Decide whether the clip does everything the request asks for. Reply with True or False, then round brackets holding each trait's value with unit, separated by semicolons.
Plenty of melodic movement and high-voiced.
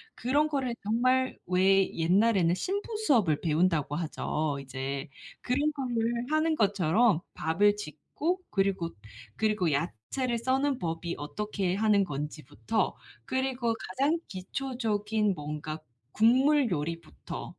True (7.5 semitones; 205 Hz)